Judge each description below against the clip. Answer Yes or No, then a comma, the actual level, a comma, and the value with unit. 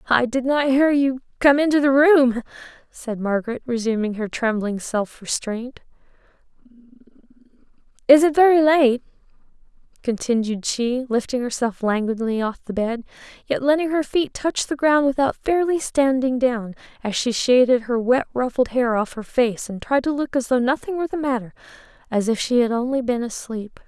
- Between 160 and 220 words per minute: Yes, average, 165 wpm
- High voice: Yes, very high, 250 Hz